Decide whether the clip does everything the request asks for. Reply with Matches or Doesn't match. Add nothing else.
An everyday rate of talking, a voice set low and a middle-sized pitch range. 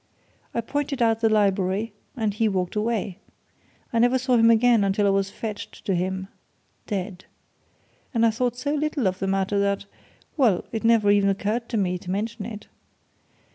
Doesn't match